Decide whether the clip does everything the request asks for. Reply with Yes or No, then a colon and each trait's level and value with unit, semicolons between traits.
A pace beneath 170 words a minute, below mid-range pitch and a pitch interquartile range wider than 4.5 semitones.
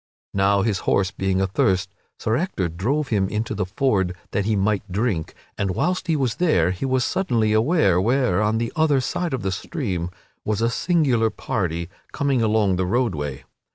No: average, 180 wpm; low, 105 Hz; wide, 5.4 semitones